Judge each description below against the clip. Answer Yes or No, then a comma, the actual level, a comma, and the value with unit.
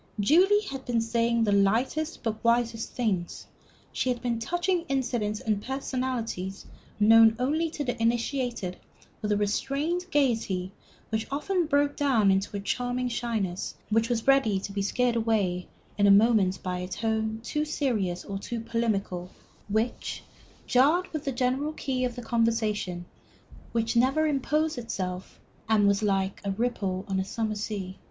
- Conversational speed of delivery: Yes, average, 160 wpm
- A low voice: No, high, 230 Hz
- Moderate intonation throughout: Yes, average, 4.3 semitones